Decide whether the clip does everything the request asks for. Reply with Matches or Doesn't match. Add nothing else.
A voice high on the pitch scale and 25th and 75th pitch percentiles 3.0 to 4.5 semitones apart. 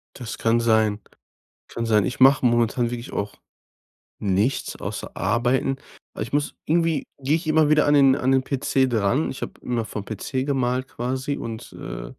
Doesn't match